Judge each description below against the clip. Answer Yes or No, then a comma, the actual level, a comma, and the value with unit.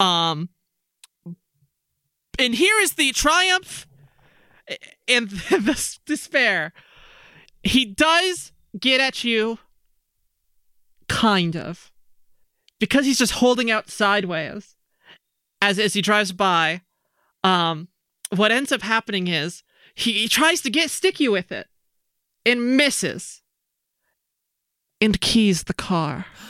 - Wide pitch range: Yes, wide, 6.8 semitones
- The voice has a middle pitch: No, high, 210 Hz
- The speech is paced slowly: Yes, slow, 105 wpm